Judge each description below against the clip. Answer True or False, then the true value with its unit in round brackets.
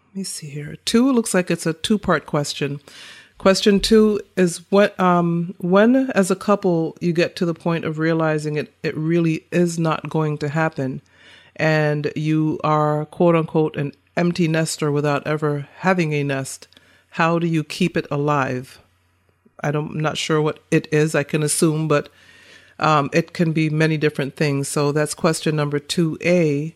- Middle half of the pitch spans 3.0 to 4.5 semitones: False (2.6 semitones)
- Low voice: False (160 Hz)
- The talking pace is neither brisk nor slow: True (180 wpm)